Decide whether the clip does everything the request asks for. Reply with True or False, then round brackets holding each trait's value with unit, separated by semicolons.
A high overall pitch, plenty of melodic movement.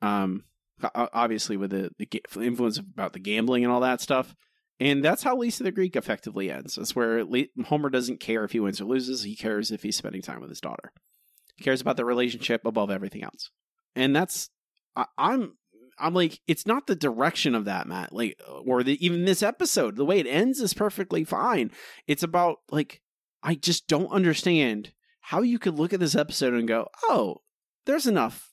False (140 Hz; 8.2 semitones)